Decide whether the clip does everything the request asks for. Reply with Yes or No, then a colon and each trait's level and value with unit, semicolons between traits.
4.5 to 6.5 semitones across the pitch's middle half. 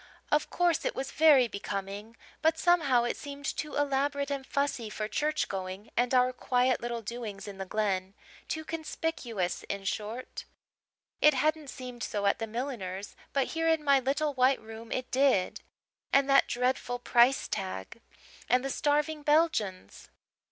Yes: average, 5.1 semitones